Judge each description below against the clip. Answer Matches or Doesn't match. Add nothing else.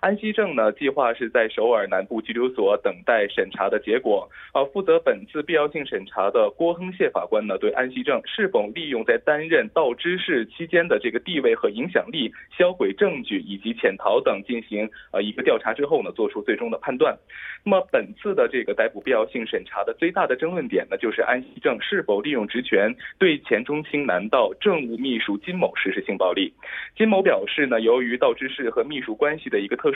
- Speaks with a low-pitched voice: Doesn't match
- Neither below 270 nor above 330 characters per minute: Matches